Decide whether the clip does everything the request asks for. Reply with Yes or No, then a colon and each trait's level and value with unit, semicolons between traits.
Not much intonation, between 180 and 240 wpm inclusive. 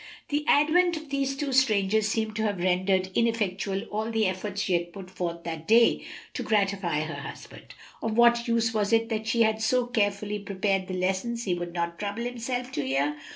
No: average, 3.8 semitones; average, 200 wpm